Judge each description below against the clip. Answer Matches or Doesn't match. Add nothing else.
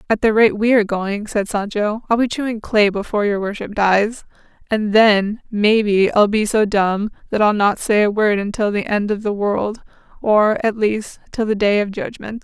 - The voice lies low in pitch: Doesn't match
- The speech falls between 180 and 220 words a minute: Matches